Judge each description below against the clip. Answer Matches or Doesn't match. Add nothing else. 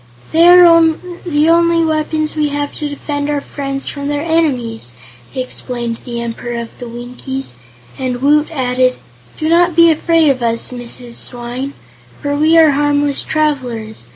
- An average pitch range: Matches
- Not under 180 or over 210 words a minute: Doesn't match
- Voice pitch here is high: Matches